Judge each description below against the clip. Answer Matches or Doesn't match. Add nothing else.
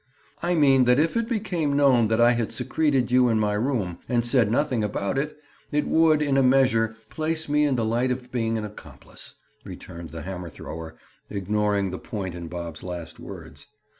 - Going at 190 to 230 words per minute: Matches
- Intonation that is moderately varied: Doesn't match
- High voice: Doesn't match